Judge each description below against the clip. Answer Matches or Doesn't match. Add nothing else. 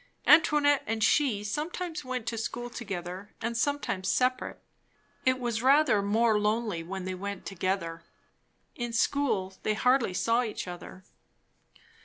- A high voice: Matches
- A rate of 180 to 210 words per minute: Doesn't match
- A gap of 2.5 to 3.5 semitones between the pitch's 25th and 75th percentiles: Doesn't match